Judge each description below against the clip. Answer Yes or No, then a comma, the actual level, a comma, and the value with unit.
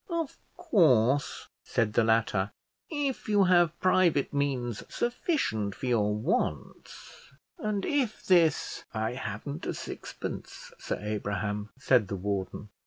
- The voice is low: Yes, low, 130 Hz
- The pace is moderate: No, slow, 125 wpm